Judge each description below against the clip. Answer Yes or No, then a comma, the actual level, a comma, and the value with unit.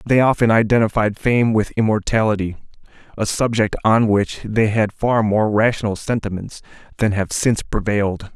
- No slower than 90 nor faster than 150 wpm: Yes, average, 145 wpm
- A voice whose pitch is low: Yes, low, 110 Hz